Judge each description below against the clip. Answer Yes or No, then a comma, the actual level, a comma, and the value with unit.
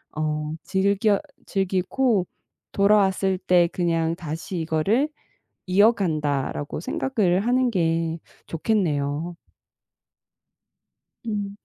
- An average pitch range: Yes, average, 3.8 semitones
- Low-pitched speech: No, medium, 185 Hz